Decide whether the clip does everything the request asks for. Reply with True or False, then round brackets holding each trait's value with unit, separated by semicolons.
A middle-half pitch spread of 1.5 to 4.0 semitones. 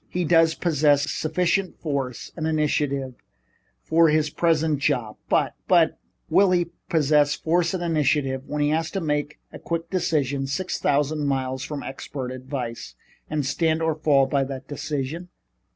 True (2.9 semitones)